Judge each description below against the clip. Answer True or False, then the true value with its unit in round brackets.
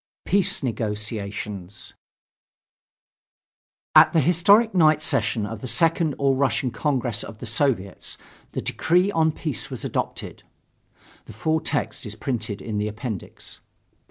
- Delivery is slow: True (130 wpm)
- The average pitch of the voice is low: True (125 Hz)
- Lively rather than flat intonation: True (6.9 semitones)